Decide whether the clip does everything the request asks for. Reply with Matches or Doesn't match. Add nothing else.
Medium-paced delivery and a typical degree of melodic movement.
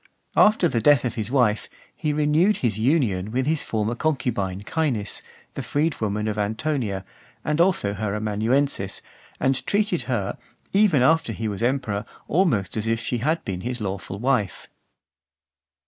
Doesn't match